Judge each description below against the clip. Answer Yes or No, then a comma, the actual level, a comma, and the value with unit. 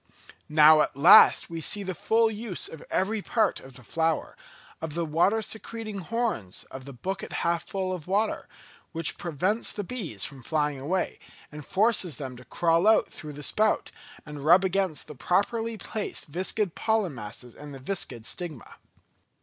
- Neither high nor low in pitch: Yes, medium, 170 Hz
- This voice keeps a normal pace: Yes, average, 170 wpm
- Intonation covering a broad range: Yes, wide, 5.7 semitones